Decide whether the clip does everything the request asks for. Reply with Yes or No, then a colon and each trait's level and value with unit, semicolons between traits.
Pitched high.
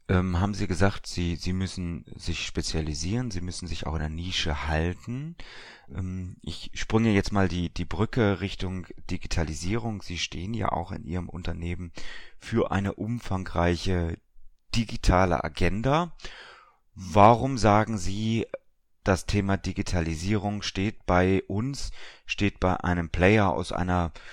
No: very low, 95 Hz